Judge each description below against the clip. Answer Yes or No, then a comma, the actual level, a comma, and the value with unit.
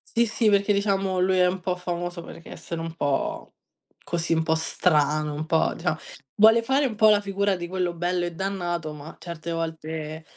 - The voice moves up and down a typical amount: Yes, average, 3.4 semitones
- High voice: No, medium, 175 Hz